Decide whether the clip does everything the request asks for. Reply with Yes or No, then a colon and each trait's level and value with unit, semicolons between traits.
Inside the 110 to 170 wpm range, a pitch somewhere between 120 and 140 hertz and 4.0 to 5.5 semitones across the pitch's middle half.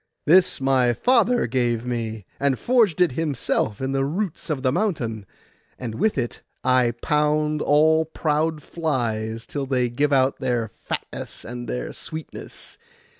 Yes: average, 145 wpm; low, 135 Hz; average, 4.7 semitones